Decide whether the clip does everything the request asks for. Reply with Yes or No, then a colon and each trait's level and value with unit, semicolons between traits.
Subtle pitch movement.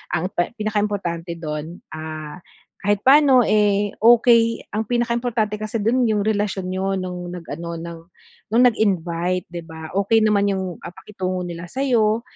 No: average, 4.2 semitones